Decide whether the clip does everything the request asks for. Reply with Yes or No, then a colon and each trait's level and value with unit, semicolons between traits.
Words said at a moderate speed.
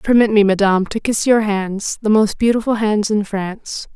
Yes: average, 195 wpm